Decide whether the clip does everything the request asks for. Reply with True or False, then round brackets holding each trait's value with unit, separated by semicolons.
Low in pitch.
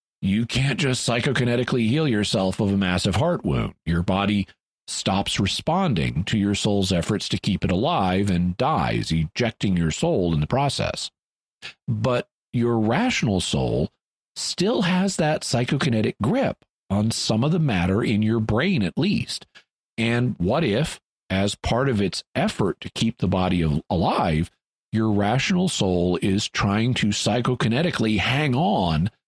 True (105 Hz)